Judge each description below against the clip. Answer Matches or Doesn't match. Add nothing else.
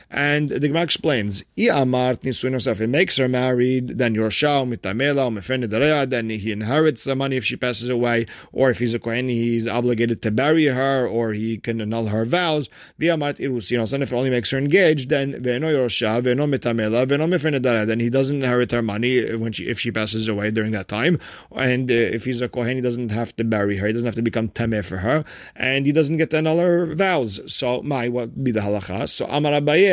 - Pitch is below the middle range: Matches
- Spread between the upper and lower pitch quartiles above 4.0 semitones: Doesn't match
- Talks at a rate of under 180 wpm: Doesn't match